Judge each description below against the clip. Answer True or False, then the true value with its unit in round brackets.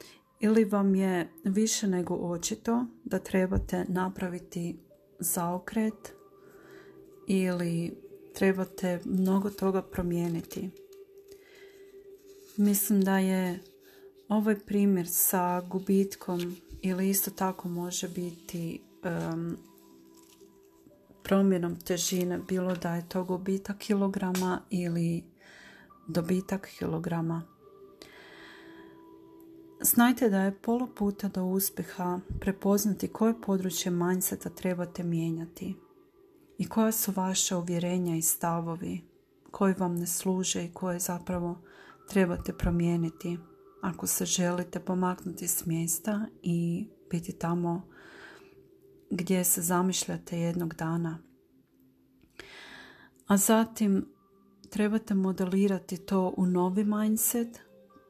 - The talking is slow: True (90 wpm)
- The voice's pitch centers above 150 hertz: True (190 Hz)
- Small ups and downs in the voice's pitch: False (3.3 semitones)